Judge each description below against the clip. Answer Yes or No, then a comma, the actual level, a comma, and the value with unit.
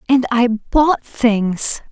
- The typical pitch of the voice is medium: No, high, 240 Hz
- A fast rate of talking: No, slow, 125 wpm